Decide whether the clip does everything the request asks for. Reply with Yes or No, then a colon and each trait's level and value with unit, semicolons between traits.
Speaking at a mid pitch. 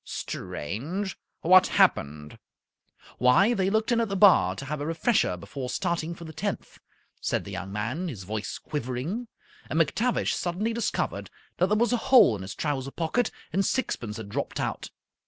Yes: medium, 165 Hz